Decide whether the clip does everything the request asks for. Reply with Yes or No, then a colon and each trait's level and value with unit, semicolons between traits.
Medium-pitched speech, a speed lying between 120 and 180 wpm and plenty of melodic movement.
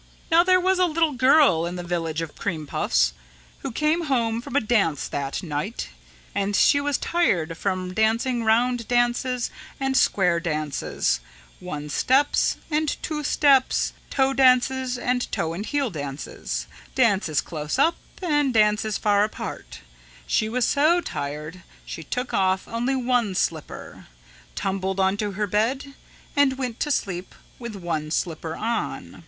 No: high, 220 Hz; average, 150 wpm; wide, 7.2 semitones